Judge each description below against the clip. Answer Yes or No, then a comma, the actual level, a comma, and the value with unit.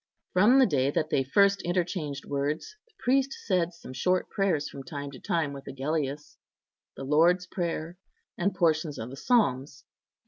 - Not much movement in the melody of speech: No, average, 4.6 semitones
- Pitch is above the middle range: No, medium, 160 Hz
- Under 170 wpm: Yes, average, 160 wpm